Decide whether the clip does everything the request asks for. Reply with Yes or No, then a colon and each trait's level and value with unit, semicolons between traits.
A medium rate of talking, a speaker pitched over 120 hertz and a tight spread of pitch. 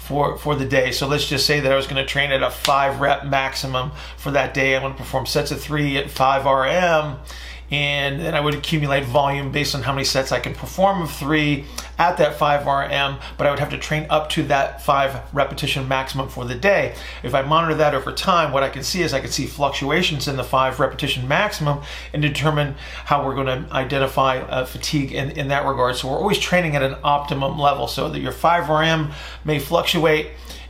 No: fast, 215 wpm; medium, 140 Hz; narrow, 1.7 semitones